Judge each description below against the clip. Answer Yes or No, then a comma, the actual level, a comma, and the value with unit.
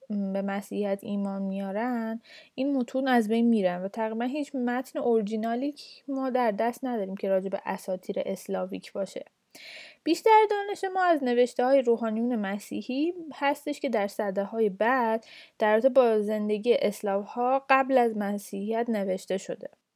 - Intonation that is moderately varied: Yes, average, 4.8 semitones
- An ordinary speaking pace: Yes, average, 140 wpm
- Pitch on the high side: Yes, high, 230 Hz